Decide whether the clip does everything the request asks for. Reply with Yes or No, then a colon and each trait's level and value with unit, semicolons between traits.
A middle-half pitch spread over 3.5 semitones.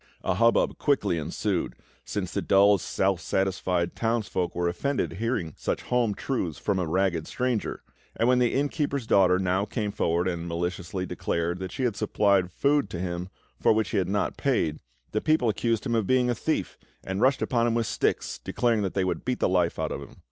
Yes: average, 4.8 semitones